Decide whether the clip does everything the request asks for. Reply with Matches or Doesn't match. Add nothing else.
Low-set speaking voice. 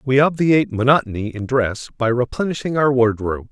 Matches